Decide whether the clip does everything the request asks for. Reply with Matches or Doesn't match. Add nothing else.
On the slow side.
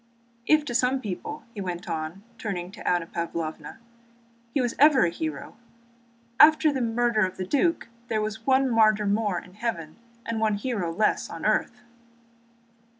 Doesn't match